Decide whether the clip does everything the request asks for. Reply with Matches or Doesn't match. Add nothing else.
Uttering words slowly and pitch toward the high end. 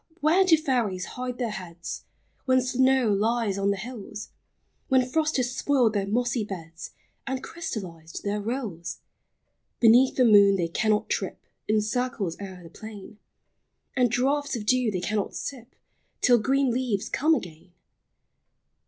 Doesn't match